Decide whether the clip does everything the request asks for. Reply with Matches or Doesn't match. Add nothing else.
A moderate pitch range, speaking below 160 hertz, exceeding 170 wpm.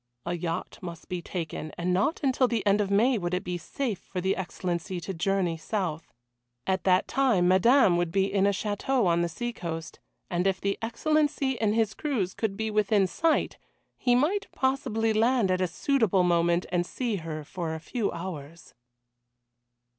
Doesn't match